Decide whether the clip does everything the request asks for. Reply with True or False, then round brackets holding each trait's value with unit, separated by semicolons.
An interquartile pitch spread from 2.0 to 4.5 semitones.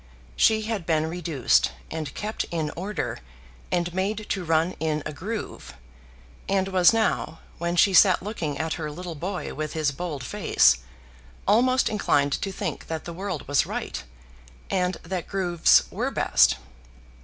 True (3.9 semitones)